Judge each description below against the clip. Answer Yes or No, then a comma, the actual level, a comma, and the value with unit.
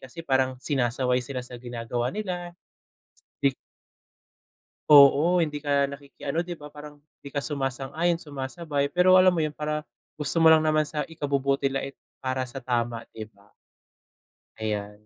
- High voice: No, medium, 140 Hz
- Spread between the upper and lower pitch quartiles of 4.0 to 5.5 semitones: No, average, 3.0 semitones